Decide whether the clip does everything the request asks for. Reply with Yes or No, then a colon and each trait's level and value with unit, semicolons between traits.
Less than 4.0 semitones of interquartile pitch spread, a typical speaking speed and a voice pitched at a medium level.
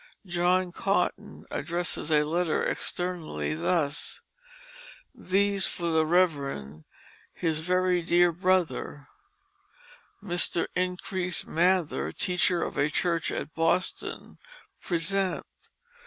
No: narrow, 2.5 semitones; slow, 95 wpm; medium, 175 Hz